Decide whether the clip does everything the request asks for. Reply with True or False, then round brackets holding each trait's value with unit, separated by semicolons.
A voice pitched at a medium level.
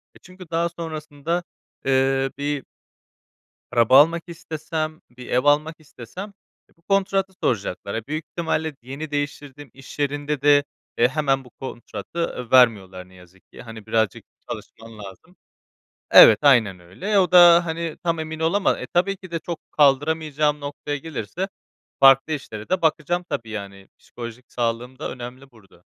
True (145 Hz)